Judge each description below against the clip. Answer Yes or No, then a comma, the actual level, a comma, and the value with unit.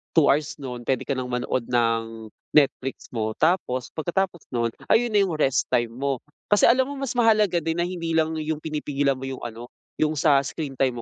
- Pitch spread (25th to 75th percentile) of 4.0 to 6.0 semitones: Yes, average, 5.3 semitones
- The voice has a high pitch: No, medium, 145 Hz